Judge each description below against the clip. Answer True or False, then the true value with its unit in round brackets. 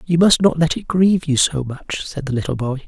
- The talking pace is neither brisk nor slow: False (270 wpm)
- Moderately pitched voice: True (155 Hz)